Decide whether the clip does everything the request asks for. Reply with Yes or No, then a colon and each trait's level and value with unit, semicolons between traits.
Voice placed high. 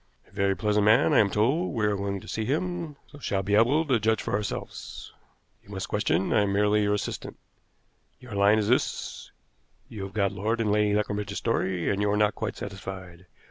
No: low, 105 Hz